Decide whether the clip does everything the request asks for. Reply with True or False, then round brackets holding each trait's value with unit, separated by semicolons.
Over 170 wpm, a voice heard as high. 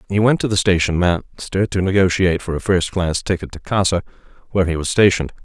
False (200 wpm; 90 Hz)